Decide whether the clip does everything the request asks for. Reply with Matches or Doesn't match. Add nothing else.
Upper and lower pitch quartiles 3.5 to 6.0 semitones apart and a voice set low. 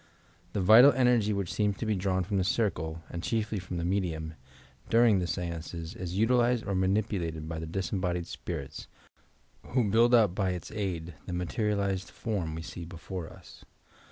Matches